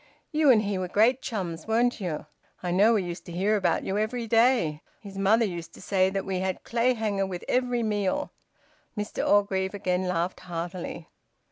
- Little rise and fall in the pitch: No, average, 3.7 semitones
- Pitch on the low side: No, high, 195 Hz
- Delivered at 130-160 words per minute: No, average, 180 wpm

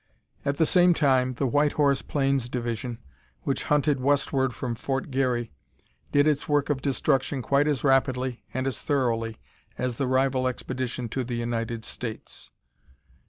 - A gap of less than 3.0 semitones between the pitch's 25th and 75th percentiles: Yes, narrow, 2.4 semitones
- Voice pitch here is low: Yes, low, 130 Hz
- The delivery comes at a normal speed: Yes, average, 155 wpm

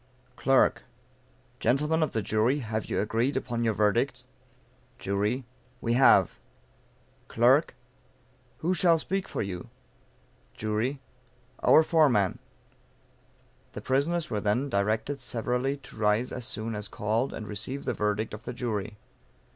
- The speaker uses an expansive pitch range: No, average, 4.3 semitones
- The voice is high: No, low, 115 Hz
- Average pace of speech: No, slow, 130 wpm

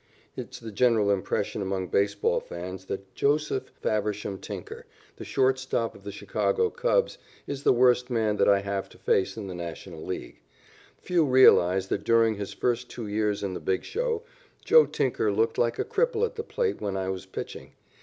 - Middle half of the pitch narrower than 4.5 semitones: No, average, 5.1 semitones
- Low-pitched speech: Yes, low, 105 Hz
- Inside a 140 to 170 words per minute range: No, average, 190 wpm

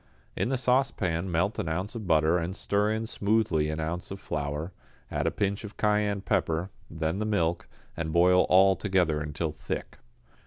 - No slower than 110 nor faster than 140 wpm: No, average, 180 wpm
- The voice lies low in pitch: Yes, very low, 90 Hz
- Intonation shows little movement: No, average, 4.2 semitones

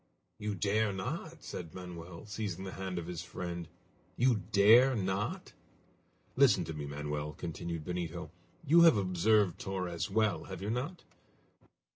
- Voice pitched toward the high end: No, very low, 95 Hz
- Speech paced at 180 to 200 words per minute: No, average, 140 wpm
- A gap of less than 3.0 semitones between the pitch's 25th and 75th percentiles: No, average, 4.1 semitones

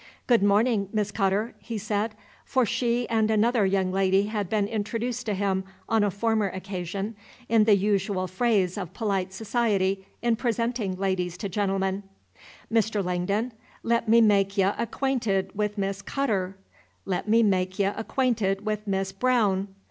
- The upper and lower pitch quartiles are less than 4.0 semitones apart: Yes, average, 2.7 semitones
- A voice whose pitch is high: Yes, high, 205 Hz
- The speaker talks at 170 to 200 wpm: No, average, 155 wpm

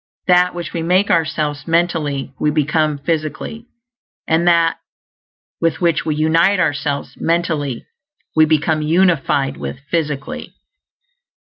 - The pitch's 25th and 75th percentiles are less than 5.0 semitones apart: Yes, narrow, 2.5 semitones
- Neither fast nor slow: No, slow, 115 wpm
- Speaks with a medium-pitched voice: Yes, medium, 160 Hz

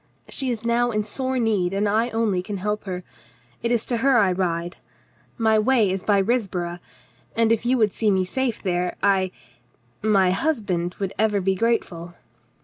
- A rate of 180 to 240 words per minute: Yes, average, 185 wpm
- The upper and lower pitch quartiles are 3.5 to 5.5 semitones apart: Yes, average, 3.8 semitones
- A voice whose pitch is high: Yes, high, 210 Hz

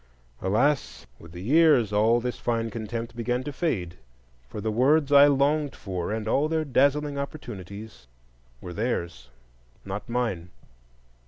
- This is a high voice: No, low, 115 Hz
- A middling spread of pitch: No, wide, 5.7 semitones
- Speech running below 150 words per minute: Yes, average, 140 wpm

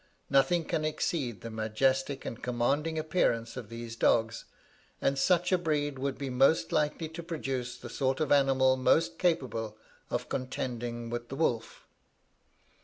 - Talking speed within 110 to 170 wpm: Yes, average, 150 wpm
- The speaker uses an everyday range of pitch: Yes, average, 4.5 semitones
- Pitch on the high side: No, low, 135 Hz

